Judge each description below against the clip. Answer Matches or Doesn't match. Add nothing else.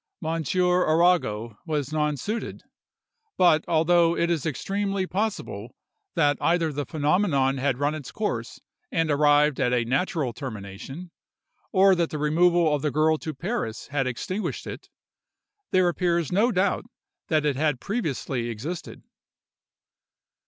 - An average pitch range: Matches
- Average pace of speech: Doesn't match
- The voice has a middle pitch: Matches